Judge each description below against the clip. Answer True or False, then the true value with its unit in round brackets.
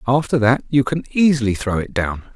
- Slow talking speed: False (205 wpm)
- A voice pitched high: False (125 Hz)